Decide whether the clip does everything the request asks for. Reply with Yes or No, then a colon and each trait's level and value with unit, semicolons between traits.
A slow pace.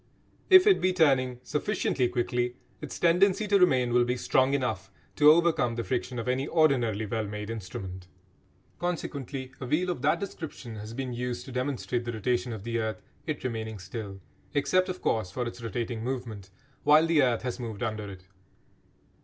No: average, 180 wpm